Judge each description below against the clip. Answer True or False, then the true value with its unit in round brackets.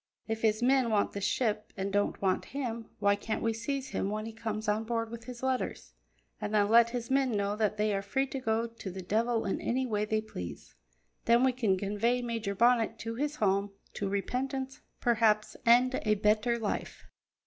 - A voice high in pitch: True (225 Hz)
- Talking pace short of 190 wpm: False (205 wpm)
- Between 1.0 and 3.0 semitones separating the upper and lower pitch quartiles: True (2.6 semitones)